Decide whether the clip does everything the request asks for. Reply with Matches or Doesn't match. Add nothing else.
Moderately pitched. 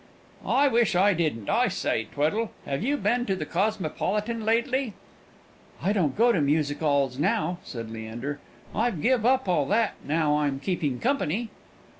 Matches